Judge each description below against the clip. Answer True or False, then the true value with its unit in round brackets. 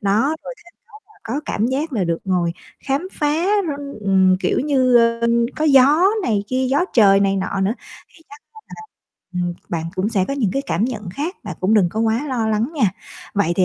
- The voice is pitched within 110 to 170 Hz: False (225 Hz)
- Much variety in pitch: True (6.4 semitones)